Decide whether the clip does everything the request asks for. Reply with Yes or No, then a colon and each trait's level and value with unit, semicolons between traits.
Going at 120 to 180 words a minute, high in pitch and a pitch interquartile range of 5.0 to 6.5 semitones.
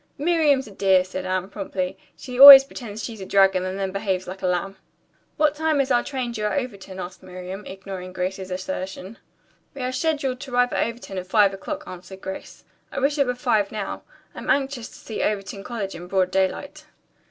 No: average, 200 wpm; high, 200 Hz; wide, 5.4 semitones